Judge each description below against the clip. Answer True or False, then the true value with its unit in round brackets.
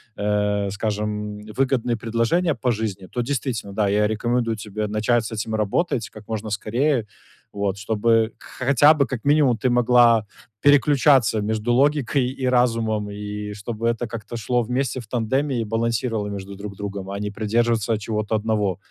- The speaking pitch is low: True (110 Hz)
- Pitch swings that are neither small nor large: True (3.0 semitones)